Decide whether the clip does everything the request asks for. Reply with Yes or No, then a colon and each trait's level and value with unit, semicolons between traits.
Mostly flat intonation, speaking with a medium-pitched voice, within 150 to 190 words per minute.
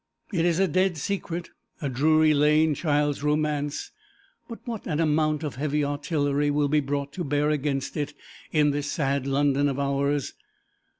Yes: narrow, 1.6 semitones; medium, 150 Hz; average, 165 wpm